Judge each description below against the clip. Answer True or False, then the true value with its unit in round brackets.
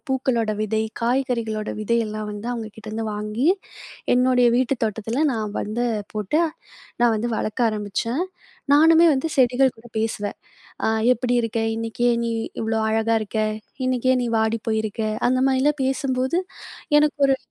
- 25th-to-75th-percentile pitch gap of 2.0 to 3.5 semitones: True (2.9 semitones)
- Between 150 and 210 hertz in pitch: False (235 Hz)